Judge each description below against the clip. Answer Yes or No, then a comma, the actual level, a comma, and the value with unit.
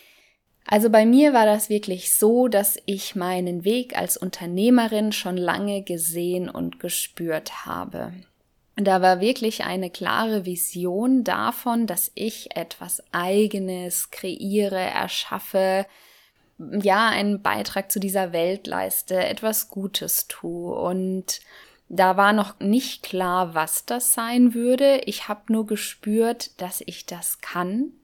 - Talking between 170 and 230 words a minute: No, average, 130 wpm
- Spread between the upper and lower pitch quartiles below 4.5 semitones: Yes, average, 3.5 semitones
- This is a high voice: Yes, high, 200 Hz